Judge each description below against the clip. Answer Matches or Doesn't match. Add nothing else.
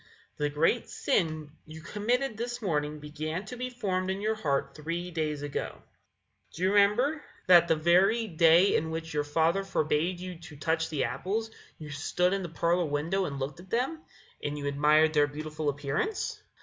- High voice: Doesn't match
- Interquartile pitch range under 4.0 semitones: Doesn't match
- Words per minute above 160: Matches